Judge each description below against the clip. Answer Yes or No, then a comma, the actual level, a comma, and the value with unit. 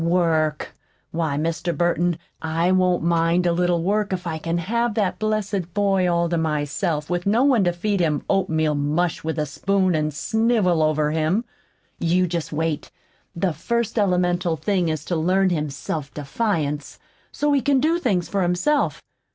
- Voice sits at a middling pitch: Yes, medium, 175 Hz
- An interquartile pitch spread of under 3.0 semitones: No, average, 3.7 semitones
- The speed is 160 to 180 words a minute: Yes, average, 170 wpm